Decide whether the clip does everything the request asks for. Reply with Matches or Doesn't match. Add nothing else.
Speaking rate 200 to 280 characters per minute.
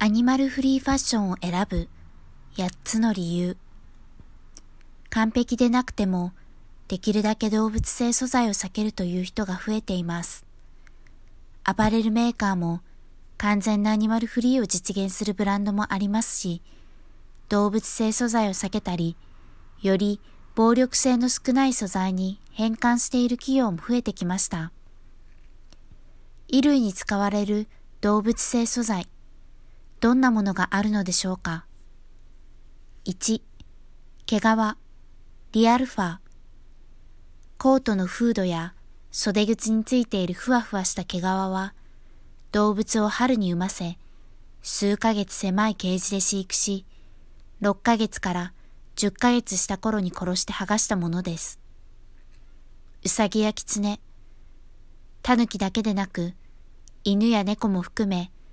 Matches